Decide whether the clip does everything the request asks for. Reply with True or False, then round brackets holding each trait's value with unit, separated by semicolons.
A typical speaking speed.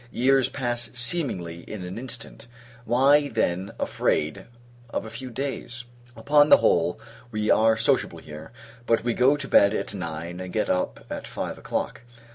True (160 wpm)